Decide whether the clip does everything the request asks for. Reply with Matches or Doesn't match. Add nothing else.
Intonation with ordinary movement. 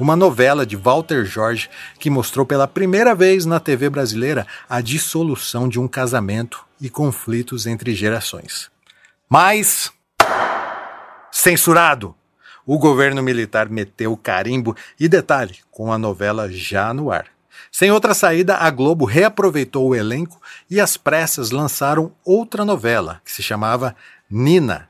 Doesn't match